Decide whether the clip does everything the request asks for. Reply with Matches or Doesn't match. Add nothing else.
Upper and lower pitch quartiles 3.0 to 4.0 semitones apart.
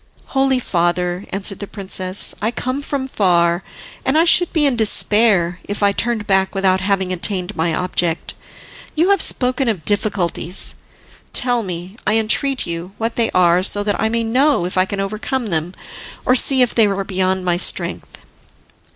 Doesn't match